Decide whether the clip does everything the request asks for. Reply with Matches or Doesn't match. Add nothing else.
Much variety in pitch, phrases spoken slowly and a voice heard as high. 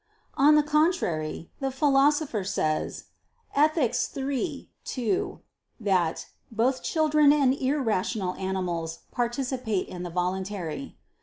Matches